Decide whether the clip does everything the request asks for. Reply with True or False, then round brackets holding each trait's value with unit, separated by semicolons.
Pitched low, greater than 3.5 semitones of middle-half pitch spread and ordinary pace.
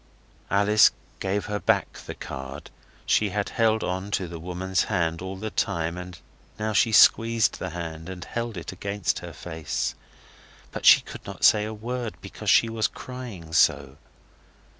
True (95 Hz; 4.2 semitones; 165 wpm)